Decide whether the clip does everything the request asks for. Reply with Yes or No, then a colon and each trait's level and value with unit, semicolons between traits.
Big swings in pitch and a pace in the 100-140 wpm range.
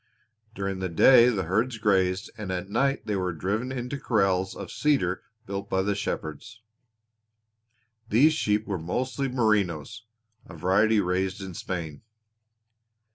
No: average, 3.6 semitones; slow, 135 wpm